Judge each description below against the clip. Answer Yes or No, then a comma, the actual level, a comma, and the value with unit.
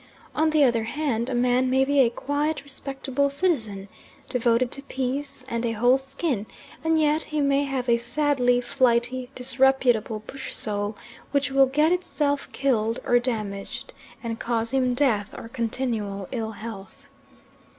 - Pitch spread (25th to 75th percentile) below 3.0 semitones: No, average, 3.3 semitones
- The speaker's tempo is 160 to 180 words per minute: No, average, 150 wpm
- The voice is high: Yes, very high, 255 Hz